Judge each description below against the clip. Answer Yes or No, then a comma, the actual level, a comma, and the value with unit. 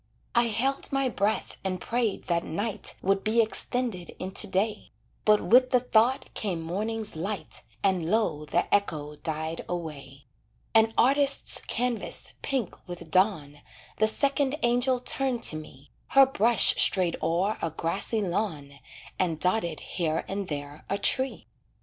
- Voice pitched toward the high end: Yes, high, 200 Hz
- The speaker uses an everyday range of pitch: No, wide, 6.1 semitones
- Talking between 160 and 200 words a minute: No, average, 145 wpm